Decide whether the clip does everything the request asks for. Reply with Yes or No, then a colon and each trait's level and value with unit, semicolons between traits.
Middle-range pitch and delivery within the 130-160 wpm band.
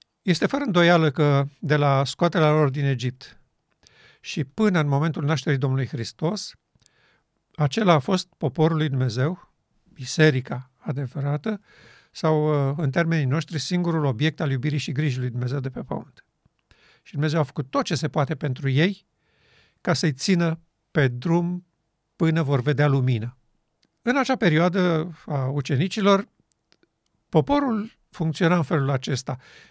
Yes: medium, 155 Hz; average, 140 wpm